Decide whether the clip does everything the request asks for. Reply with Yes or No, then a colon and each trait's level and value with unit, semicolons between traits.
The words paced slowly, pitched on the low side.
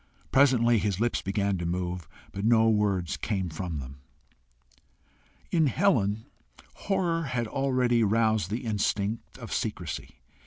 Yes: slow, 125 wpm; low, 110 Hz